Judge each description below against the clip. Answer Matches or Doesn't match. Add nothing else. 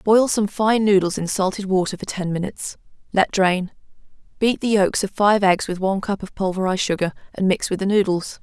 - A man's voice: Doesn't match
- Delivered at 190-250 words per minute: Matches